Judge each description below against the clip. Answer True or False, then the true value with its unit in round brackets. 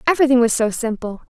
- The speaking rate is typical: True (180 wpm)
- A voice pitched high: True (240 Hz)